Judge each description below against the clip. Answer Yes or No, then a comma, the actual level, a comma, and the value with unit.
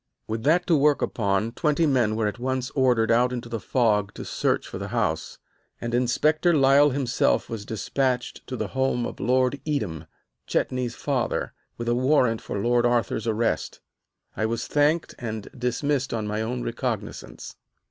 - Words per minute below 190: Yes, average, 170 wpm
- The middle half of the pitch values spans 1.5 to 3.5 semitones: Yes, average, 3.0 semitones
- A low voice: Yes, low, 125 Hz